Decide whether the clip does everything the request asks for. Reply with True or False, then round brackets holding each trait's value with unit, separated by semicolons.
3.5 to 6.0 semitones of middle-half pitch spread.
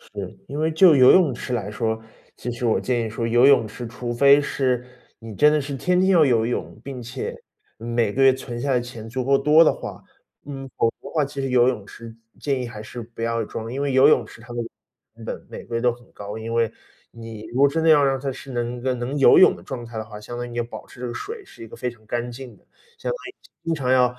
False (3.0 semitones)